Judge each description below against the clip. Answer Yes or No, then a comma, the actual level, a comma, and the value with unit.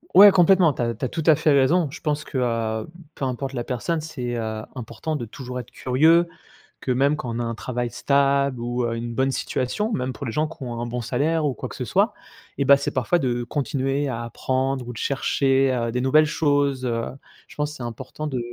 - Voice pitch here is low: Yes, low, 130 Hz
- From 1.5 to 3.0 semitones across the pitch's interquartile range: No, average, 3.4 semitones